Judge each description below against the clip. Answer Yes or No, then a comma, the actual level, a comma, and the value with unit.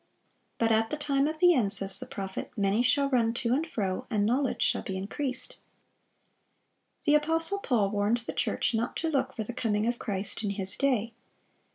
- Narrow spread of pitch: No, average, 5.2 semitones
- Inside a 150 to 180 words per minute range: No, average, 195 wpm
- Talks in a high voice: Yes, high, 235 Hz